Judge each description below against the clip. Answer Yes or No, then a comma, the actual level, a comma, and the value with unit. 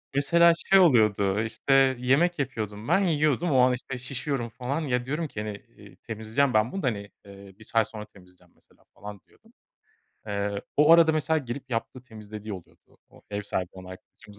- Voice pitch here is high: No, low, 120 Hz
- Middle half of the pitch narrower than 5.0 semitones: No, average, 5.3 semitones